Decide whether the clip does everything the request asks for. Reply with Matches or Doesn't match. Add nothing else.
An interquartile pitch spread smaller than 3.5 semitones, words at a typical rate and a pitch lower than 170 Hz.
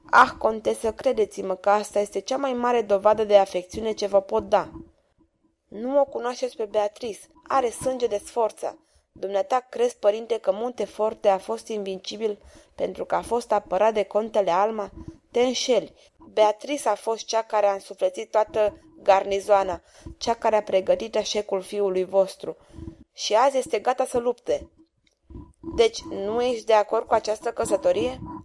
Doesn't match